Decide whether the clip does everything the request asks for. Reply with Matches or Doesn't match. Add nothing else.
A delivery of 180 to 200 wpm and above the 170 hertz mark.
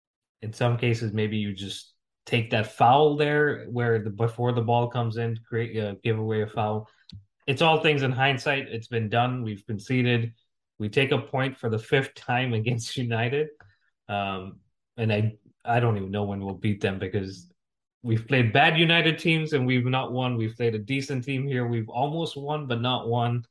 Doesn't match